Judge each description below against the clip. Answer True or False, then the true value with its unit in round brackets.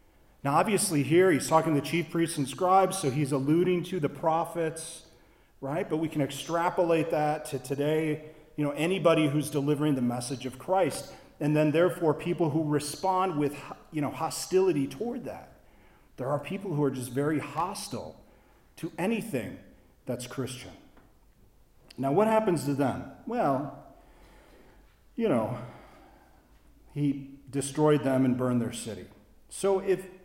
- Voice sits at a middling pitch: True (150 Hz)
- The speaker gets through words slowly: False (150 wpm)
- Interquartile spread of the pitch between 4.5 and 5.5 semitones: False (3.6 semitones)